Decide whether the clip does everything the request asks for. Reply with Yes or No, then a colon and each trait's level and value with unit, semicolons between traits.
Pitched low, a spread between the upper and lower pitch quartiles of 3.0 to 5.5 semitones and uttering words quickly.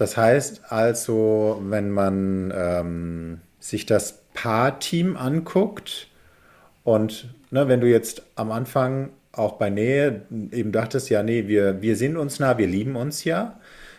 No: low, 115 Hz; average, 4.7 semitones; average, 140 wpm